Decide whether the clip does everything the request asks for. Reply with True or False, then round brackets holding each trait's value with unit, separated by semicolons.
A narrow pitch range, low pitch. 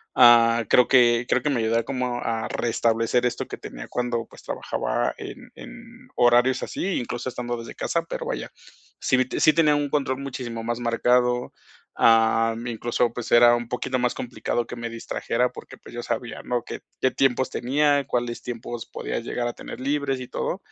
True (1.6 semitones; 120 Hz)